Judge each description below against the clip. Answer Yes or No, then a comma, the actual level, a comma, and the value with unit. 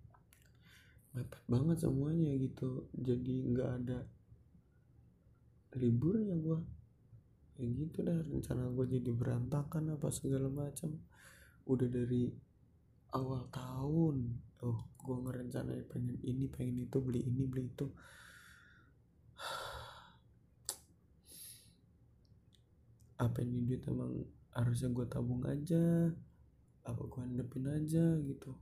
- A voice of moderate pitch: No, low, 125 Hz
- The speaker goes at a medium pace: Yes, average, 100 wpm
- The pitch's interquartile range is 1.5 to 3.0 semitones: Yes, narrow, 2.6 semitones